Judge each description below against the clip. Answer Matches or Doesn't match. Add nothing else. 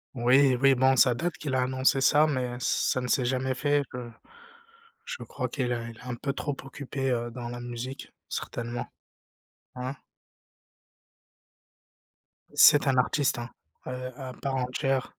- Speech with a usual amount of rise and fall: Doesn't match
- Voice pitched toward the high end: Doesn't match